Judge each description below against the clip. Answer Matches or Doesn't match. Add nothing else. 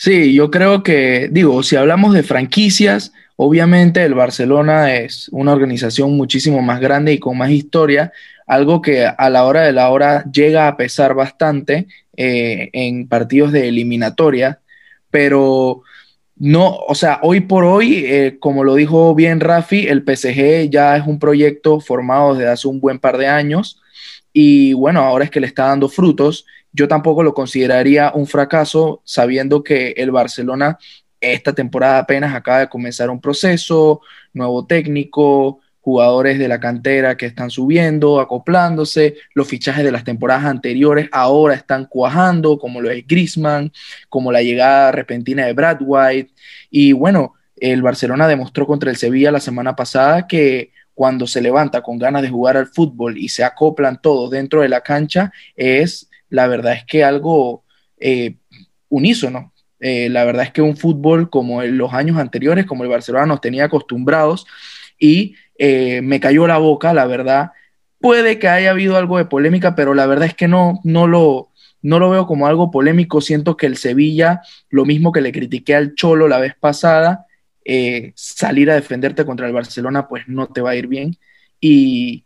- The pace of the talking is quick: Doesn't match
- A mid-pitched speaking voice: Matches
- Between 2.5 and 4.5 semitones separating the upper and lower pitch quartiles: Matches